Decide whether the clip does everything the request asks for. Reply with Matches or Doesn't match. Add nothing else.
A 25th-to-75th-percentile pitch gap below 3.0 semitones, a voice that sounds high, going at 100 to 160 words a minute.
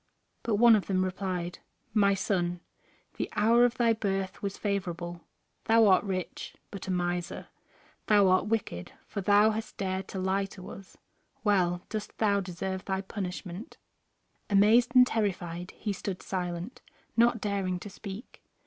Matches